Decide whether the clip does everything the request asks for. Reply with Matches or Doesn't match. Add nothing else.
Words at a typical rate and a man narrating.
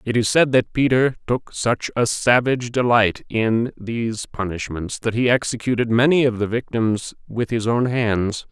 Matches